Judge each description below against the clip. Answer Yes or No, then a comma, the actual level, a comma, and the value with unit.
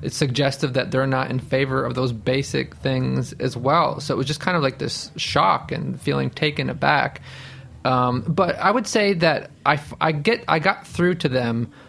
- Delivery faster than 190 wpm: Yes, average, 200 wpm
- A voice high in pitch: No, low, 135 Hz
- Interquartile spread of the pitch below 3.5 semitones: No, average, 4.0 semitones